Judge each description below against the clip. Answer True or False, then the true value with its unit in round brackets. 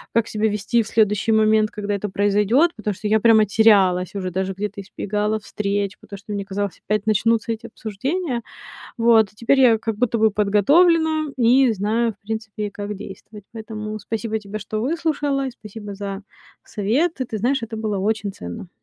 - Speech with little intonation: True (2.2 semitones)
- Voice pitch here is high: True (215 Hz)